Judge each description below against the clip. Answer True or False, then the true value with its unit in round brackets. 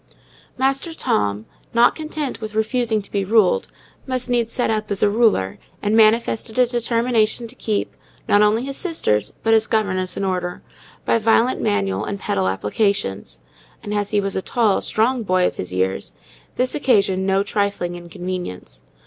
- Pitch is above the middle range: True (210 Hz)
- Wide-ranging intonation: False (4.2 semitones)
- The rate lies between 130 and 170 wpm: True (165 wpm)